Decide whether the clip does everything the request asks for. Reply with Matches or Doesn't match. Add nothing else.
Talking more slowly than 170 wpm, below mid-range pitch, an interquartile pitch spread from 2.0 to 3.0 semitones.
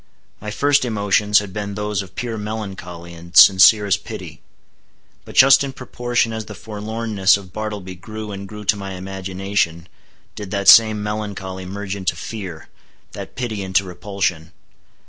Matches